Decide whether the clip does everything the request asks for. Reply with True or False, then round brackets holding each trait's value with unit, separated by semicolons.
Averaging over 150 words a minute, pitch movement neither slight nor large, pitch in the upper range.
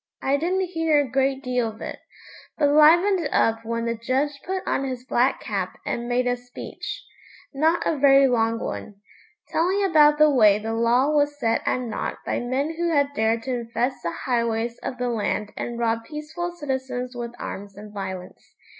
True (185 wpm; 4.4 semitones; 255 Hz)